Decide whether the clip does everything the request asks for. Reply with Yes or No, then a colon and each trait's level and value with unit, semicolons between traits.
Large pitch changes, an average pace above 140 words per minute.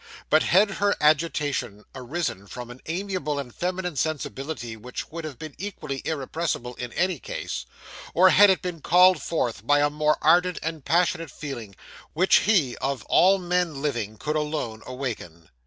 Yes: wide, 5.7 semitones; average, 160 wpm